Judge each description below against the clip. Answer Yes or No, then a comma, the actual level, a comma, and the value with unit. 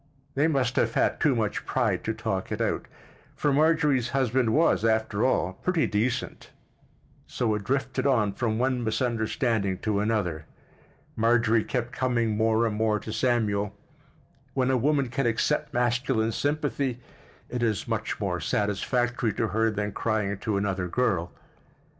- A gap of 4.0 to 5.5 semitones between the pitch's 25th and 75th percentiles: No, average, 3.3 semitones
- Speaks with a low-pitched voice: Yes, low, 115 Hz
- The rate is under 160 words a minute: Yes, average, 145 wpm